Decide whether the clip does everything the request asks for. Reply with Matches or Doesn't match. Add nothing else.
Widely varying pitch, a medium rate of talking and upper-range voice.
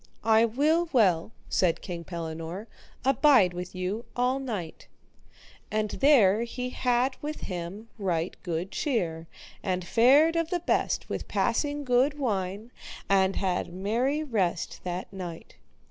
Doesn't match